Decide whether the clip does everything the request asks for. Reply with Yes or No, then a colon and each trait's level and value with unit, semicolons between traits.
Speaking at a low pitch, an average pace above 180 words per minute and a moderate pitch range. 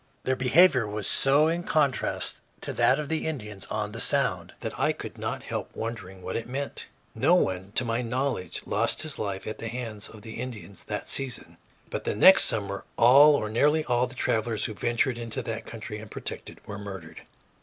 Yes: low, 115 Hz; average, 195 wpm; average, 4.1 semitones